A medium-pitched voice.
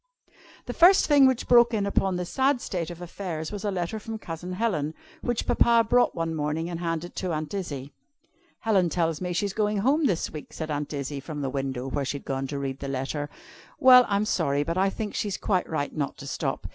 Yes: medium, 175 Hz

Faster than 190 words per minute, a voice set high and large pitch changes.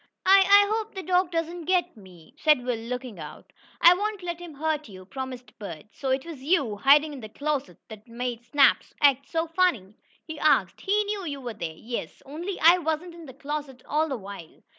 Yes: fast, 205 wpm; very high, 290 Hz; wide, 6.0 semitones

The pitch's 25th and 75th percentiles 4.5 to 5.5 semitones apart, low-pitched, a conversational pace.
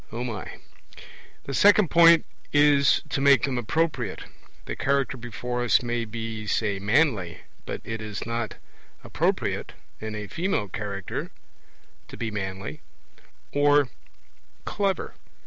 No: average, 4.9 semitones; low, 120 Hz; slow, 115 wpm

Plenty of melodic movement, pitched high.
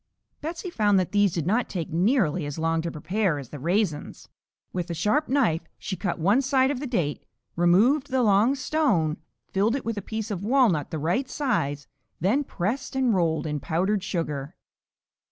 Yes: wide, 7.4 semitones; high, 195 Hz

